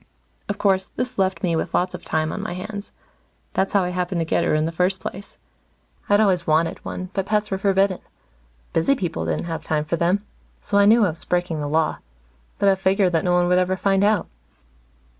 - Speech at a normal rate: No, fast, 220 wpm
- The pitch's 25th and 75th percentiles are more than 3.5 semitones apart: No, average, 3.0 semitones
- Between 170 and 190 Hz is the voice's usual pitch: Yes, medium, 185 Hz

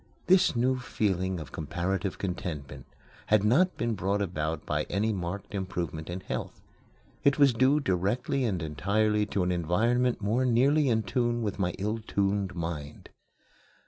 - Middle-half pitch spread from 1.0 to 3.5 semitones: No, average, 4.9 semitones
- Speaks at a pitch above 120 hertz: No, low, 100 Hz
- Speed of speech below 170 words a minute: Yes, average, 150 wpm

